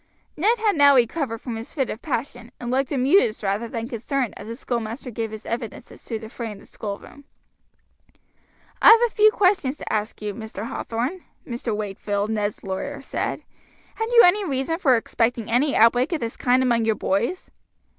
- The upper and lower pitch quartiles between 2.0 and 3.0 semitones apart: No, average, 4.3 semitones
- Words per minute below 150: No, average, 190 wpm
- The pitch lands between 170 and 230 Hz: No, high, 240 Hz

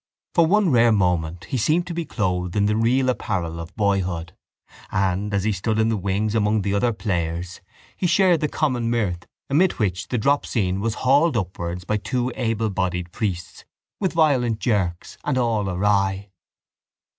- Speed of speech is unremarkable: Yes, average, 170 wpm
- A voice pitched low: Yes, low, 105 Hz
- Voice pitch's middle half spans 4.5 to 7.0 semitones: Yes, average, 5.2 semitones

